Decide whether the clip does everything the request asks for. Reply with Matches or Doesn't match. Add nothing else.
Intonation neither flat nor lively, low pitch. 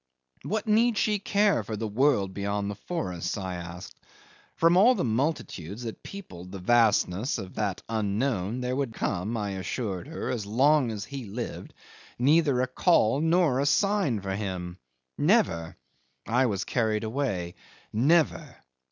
Doesn't match